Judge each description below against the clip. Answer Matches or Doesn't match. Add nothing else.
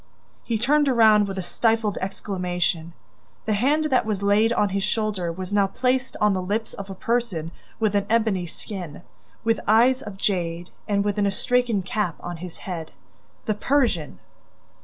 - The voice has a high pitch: Matches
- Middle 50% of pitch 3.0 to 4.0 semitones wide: Matches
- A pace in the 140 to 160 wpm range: Doesn't match